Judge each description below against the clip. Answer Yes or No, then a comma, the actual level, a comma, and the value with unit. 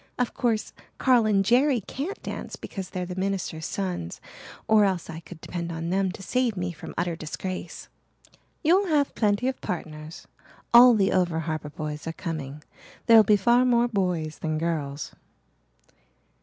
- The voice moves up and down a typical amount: No, wide, 6.1 semitones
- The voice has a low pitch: No, medium, 185 Hz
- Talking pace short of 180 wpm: Yes, average, 160 wpm